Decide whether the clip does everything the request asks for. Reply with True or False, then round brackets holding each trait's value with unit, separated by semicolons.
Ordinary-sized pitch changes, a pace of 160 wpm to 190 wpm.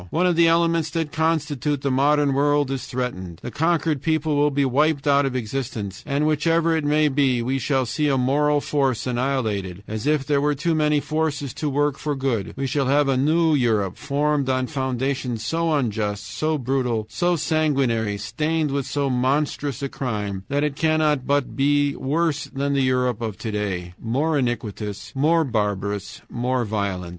True (3.7 semitones; 180 wpm)